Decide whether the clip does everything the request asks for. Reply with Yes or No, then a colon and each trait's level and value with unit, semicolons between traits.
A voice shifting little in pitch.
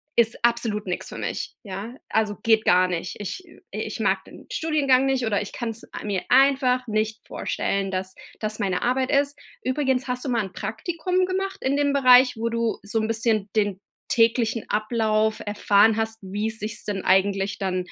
No: average, 3.7 semitones